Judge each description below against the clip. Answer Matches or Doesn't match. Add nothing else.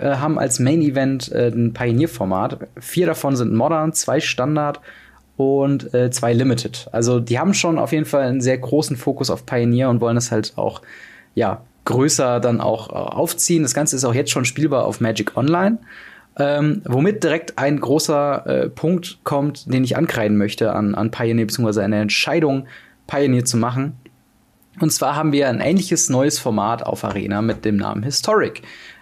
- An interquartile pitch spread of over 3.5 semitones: Matches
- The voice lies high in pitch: Doesn't match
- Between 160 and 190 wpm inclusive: Matches